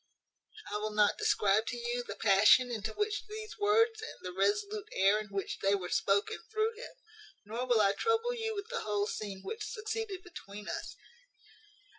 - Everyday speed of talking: Yes, average, 180 wpm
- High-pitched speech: Yes, high, 245 Hz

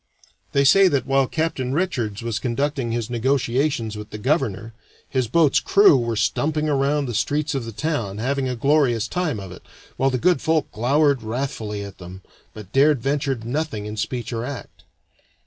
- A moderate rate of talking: Yes, average, 180 wpm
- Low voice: Yes, low, 130 Hz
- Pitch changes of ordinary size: Yes, average, 4.3 semitones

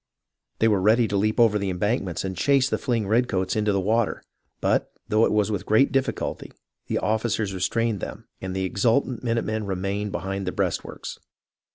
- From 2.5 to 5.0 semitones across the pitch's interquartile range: Yes, average, 2.9 semitones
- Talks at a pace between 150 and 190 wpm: Yes, average, 185 wpm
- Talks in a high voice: No, low, 105 Hz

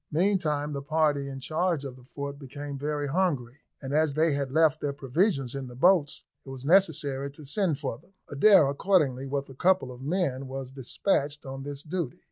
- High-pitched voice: No, medium, 145 Hz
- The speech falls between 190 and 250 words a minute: Yes, average, 195 wpm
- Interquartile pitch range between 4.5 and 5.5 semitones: No, average, 2.9 semitones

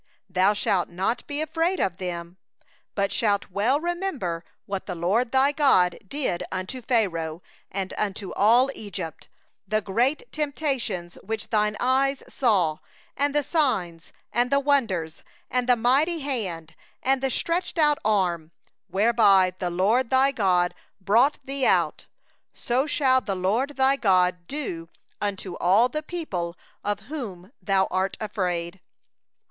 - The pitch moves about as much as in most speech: No, wide, 6.5 semitones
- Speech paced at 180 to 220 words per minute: No, average, 140 wpm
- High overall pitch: Yes, high, 210 Hz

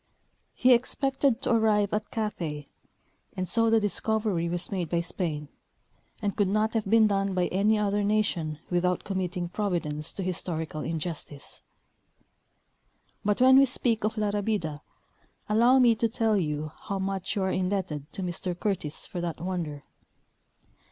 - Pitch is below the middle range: No, high, 195 Hz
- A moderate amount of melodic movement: Yes, average, 3.9 semitones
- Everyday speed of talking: Yes, average, 155 wpm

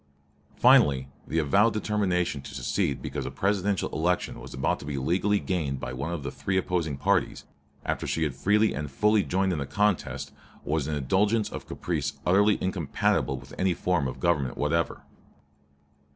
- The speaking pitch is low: Yes, very low, 85 Hz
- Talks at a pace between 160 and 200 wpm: Yes, average, 170 wpm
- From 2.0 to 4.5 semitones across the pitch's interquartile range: No, wide, 5.4 semitones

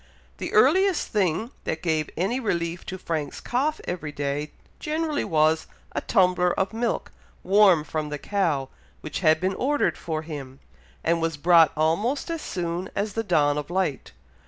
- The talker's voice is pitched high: No, medium, 175 Hz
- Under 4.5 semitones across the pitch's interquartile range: No, average, 5.1 semitones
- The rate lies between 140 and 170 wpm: Yes, average, 160 wpm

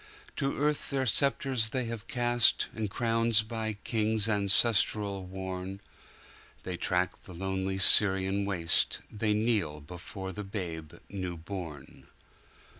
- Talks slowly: Yes, slow, 115 wpm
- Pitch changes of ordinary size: Yes, average, 3.3 semitones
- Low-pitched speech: Yes, low, 100 Hz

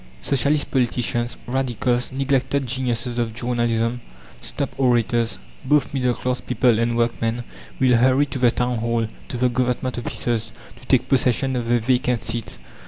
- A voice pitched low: Yes, low, 125 Hz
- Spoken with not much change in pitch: Yes, narrow, 1.6 semitones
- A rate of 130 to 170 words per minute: Yes, average, 150 wpm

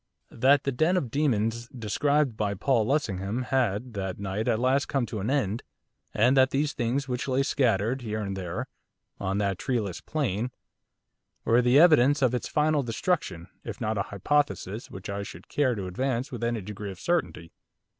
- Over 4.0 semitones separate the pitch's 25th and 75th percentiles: Yes, average, 5.0 semitones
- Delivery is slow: No, average, 180 wpm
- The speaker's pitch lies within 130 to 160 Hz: No, low, 120 Hz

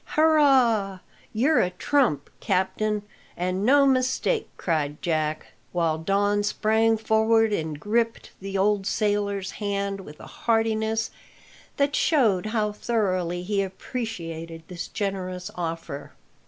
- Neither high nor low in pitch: No, high, 205 Hz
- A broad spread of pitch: No, average, 3.7 semitones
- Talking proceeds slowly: Yes, slow, 115 wpm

